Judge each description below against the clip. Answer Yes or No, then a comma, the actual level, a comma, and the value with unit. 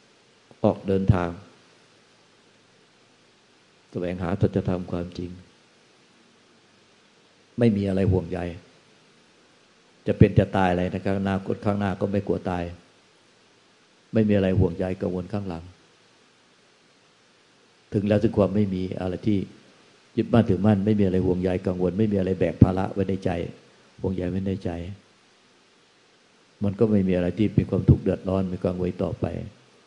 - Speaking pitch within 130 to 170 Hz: No, very low, 95 Hz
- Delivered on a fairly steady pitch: Yes, narrow, 2.1 semitones